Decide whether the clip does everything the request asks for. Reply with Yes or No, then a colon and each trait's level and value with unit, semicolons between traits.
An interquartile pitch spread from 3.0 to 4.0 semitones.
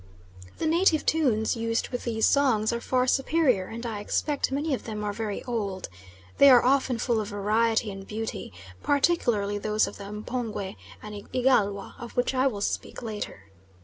Yes: average, 3.7 semitones